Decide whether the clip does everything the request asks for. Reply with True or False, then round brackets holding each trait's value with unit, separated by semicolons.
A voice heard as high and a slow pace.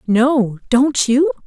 True (245 Hz; 125 wpm)